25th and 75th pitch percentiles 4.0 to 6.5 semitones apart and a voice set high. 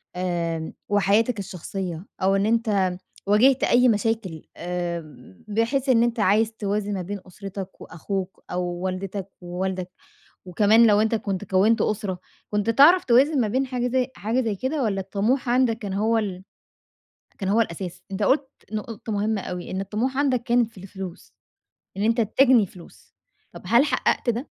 No: average, 3.6 semitones; high, 205 Hz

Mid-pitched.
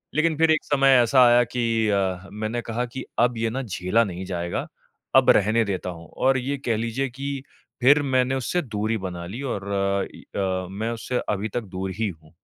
No: low, 115 Hz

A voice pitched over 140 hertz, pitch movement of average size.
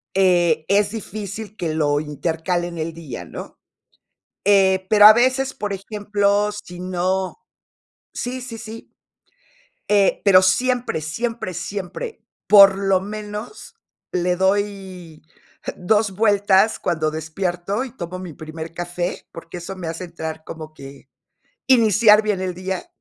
Yes: high, 190 Hz; average, 3.4 semitones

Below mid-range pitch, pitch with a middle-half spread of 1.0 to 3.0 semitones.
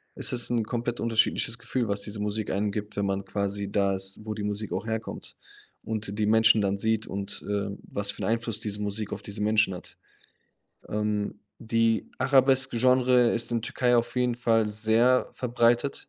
Yes: low, 110 Hz; narrow, 2.4 semitones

